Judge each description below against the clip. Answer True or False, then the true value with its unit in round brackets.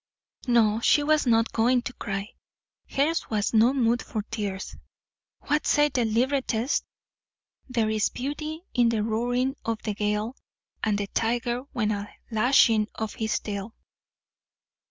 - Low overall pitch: False (230 Hz)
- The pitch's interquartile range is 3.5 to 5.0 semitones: False (2.9 semitones)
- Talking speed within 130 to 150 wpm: True (140 wpm)